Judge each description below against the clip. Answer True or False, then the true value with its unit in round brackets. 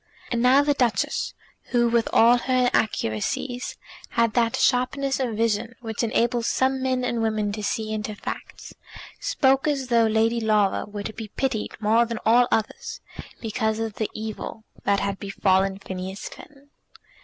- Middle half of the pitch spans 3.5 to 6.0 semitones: False (2.7 semitones)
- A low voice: False (230 Hz)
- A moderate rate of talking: True (160 wpm)